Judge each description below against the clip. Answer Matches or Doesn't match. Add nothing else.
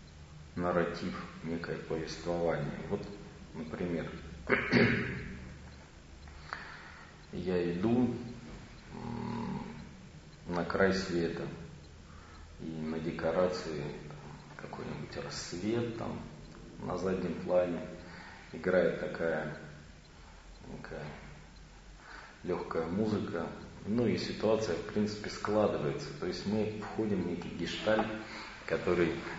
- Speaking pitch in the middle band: Doesn't match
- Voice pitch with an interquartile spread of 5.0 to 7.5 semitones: Doesn't match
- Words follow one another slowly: Matches